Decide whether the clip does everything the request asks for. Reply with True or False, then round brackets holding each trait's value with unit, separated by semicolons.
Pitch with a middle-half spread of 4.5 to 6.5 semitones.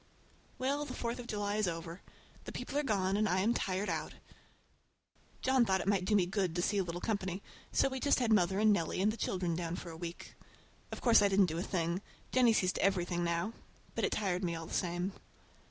False (3.5 semitones)